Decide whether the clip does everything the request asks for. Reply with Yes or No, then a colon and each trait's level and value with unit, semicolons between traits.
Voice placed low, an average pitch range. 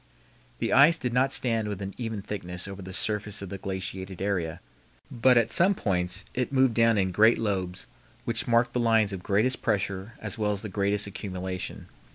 Yes: low, 105 Hz; average, 3.4 semitones